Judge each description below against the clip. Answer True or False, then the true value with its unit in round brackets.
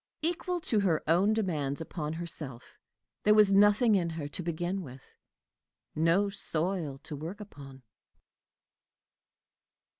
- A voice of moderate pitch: True (170 Hz)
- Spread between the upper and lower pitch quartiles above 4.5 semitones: True (5.0 semitones)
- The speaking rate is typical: False (120 wpm)